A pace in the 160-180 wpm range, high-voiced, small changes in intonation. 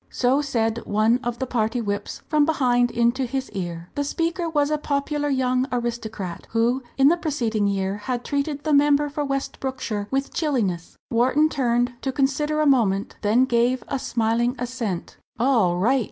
No: average, 170 wpm; very high, 250 Hz; average, 3.8 semitones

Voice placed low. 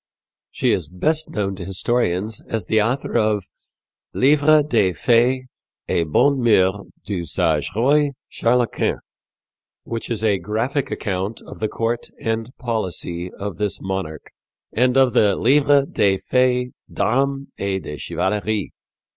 Yes: low, 110 Hz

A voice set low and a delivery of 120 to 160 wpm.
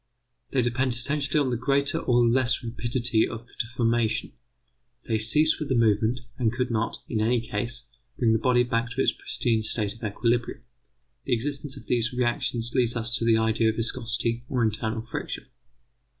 No: low, 120 Hz; average, 180 wpm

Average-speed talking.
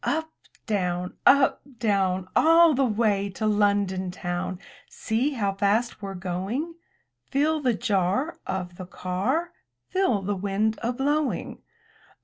No: slow, 130 wpm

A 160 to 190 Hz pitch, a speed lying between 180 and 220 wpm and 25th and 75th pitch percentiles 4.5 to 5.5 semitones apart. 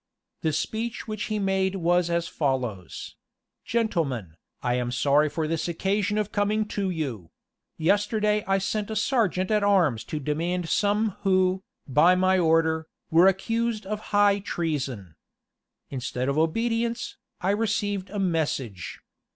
No: medium, 185 Hz; average, 140 wpm; average, 5.2 semitones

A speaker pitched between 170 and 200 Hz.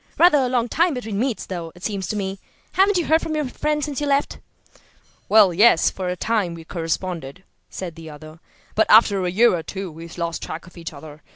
Yes: high, 190 Hz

